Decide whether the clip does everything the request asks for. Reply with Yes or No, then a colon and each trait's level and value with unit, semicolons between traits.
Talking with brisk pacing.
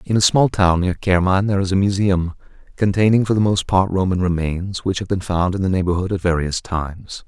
Yes: fast, 225 wpm